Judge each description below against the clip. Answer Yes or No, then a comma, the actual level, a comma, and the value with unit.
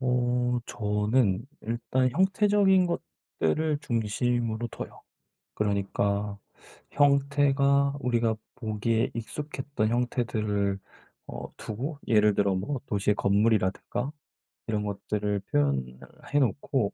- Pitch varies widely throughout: No, average, 5.0 semitones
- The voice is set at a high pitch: No, low, 115 Hz